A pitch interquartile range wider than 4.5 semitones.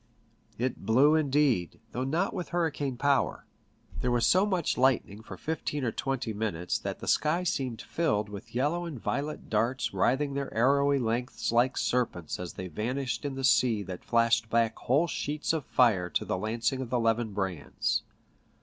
No: average, 4.2 semitones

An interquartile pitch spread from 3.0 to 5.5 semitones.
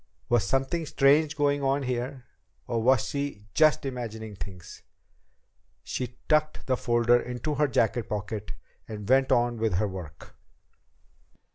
Yes: average, 4.2 semitones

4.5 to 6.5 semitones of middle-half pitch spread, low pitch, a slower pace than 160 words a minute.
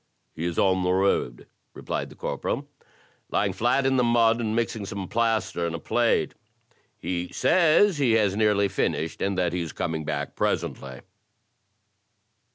No: average, 5.1 semitones; low, 100 Hz; average, 165 wpm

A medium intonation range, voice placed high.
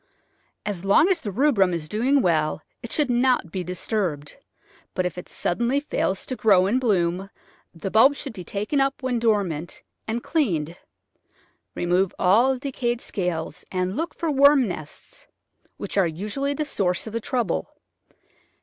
No: wide, 6.4 semitones; high, 210 Hz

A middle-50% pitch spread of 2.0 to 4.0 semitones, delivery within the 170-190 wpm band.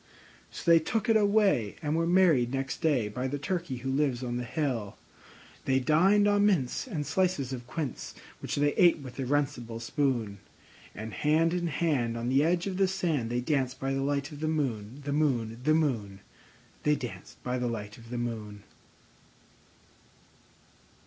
No: average, 5.0 semitones; average, 180 wpm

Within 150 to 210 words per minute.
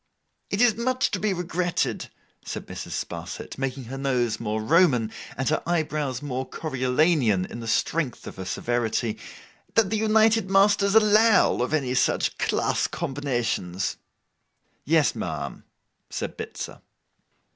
No: slow, 135 wpm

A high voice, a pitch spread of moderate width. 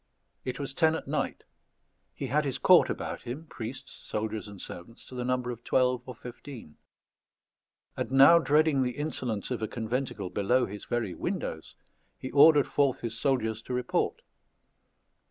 No: low, 125 Hz; average, 3.7 semitones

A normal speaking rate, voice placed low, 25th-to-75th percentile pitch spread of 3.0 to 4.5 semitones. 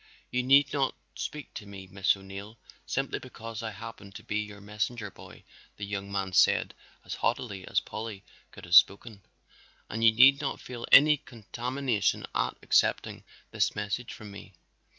Yes: average, 165 wpm; low, 105 Hz; average, 3.6 semitones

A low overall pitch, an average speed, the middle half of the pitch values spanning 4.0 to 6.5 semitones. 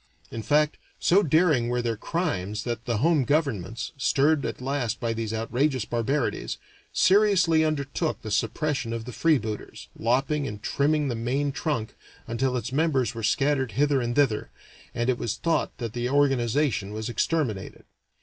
Yes: low, 130 Hz; average, 160 wpm; average, 4.4 semitones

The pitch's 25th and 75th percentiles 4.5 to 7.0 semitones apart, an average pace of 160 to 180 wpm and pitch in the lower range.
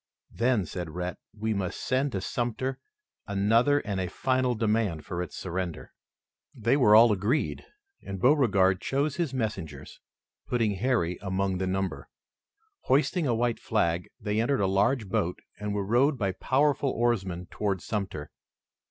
No: average, 4.8 semitones; average, 150 wpm; low, 105 Hz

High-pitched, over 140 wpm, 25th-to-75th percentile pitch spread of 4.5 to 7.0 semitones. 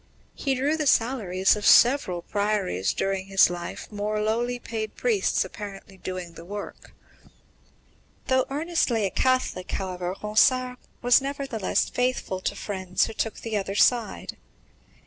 No: high, 215 Hz; slow, 135 wpm; average, 5.0 semitones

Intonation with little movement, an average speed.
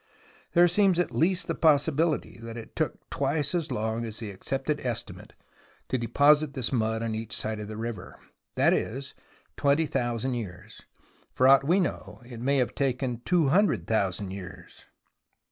No: average, 5.2 semitones; average, 165 wpm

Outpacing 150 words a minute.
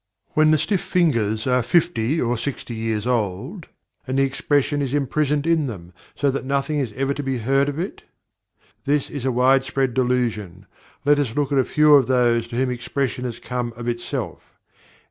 Yes: average, 190 wpm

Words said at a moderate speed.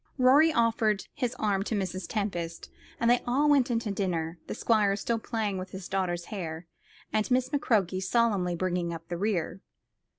Yes: average, 175 wpm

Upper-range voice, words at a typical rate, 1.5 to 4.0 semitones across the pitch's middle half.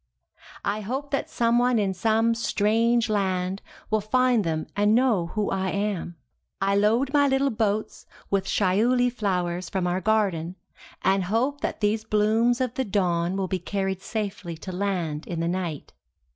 Yes: high, 205 Hz; average, 160 wpm; average, 3.6 semitones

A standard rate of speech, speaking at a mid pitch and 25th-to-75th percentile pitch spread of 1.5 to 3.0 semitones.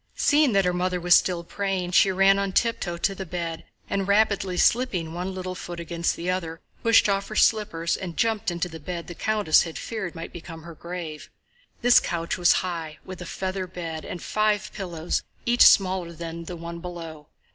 Yes: average, 195 wpm; medium, 180 Hz; narrow, 2.6 semitones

